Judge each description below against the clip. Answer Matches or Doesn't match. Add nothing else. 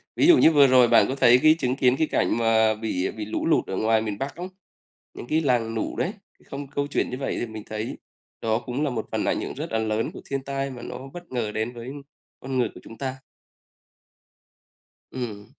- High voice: Doesn't match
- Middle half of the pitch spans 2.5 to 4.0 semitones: Matches